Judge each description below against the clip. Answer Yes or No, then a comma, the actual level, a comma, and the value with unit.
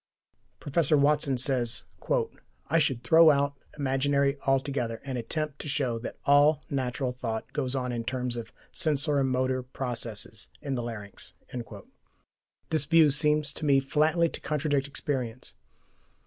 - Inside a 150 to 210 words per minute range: No, slow, 135 wpm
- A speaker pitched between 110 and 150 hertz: Yes, low, 135 Hz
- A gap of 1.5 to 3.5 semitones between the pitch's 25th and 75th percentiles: Yes, average, 2.9 semitones